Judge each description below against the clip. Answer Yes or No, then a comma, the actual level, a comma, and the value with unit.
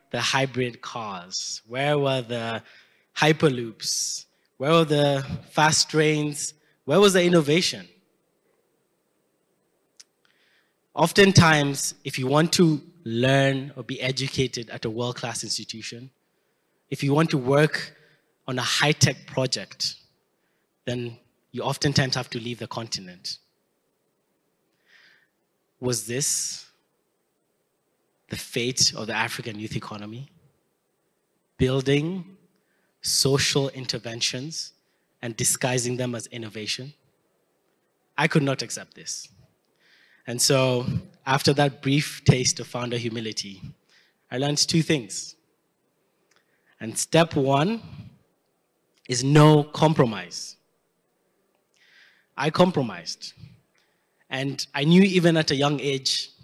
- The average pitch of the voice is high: No, medium, 140 Hz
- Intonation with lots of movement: No, average, 3.7 semitones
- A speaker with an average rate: No, slow, 105 wpm